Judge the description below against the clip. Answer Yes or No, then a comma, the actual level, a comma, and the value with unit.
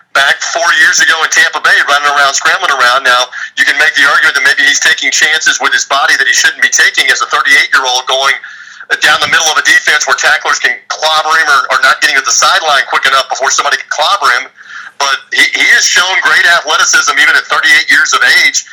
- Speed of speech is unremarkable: No, fast, 235 wpm